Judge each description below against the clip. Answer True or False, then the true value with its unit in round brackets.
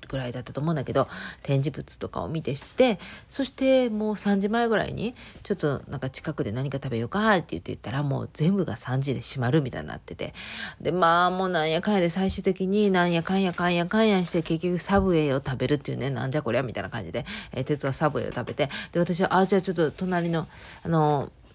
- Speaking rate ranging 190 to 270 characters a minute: False (470 characters per minute)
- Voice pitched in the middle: True (165 Hz)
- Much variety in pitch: True (5.7 semitones)